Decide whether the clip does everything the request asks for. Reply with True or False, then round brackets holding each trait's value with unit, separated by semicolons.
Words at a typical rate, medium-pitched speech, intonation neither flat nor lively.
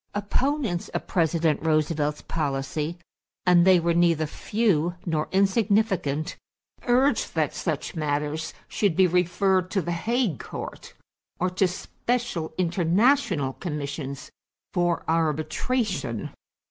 False (110 wpm; 175 Hz; 4.1 semitones)